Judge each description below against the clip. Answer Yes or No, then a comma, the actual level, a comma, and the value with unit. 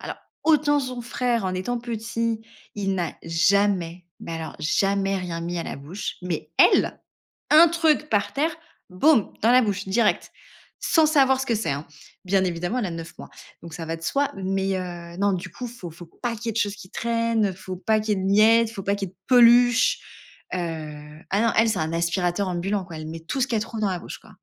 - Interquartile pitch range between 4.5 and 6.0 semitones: Yes, average, 5.0 semitones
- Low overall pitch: No, high, 200 Hz